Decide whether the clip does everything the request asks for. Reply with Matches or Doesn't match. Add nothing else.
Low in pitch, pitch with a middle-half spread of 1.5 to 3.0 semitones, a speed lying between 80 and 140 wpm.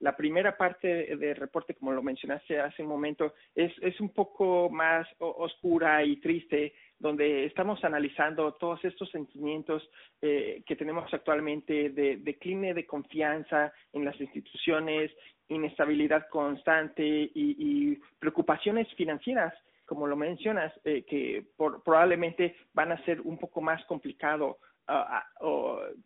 Doesn't match